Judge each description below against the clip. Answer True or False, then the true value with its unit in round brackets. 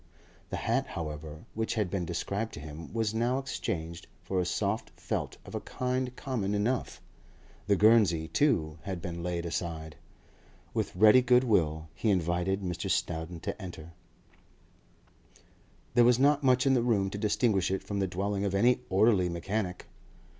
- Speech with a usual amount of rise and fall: True (5.0 semitones)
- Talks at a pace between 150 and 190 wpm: True (160 wpm)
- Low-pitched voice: True (100 Hz)